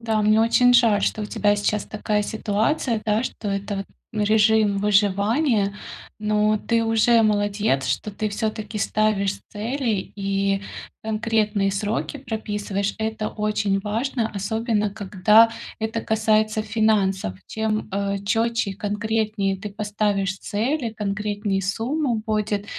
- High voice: Yes, high, 210 Hz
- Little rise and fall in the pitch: Yes, narrow, 1.6 semitones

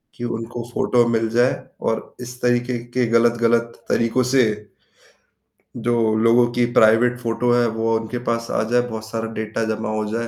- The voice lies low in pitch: Yes, low, 115 Hz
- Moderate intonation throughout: No, narrow, 1.2 semitones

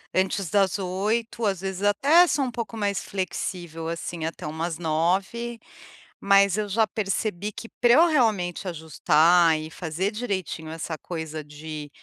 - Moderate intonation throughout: Yes, average, 4.5 semitones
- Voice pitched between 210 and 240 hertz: No, high, 190 Hz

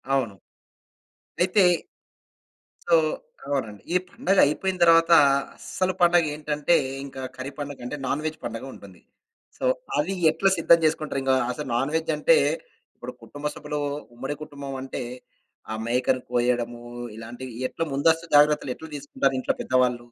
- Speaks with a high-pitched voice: No, medium, 145 Hz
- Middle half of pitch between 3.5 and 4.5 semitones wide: Yes, average, 4.1 semitones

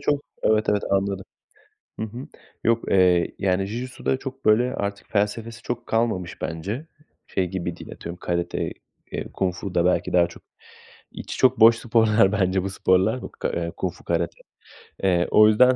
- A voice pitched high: No, low, 100 Hz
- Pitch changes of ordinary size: Yes, average, 3.9 semitones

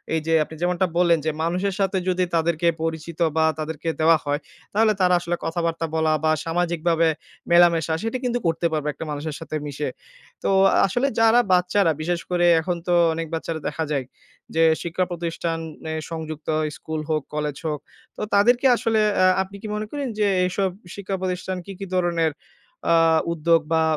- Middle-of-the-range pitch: Yes, medium, 170 Hz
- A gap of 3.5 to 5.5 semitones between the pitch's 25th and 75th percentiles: No, narrow, 2.4 semitones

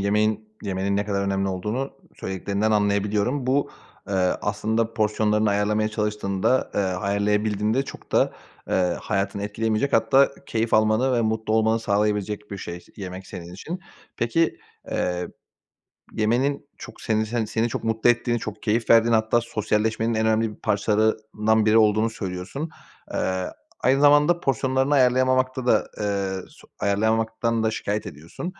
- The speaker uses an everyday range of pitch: No, narrow, 2.3 semitones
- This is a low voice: Yes, low, 110 Hz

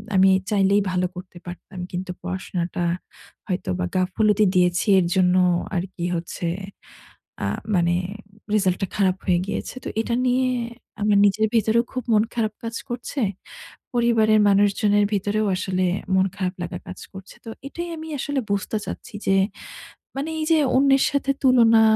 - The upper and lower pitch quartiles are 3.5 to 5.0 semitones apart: Yes, average, 3.8 semitones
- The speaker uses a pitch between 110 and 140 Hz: No, high, 205 Hz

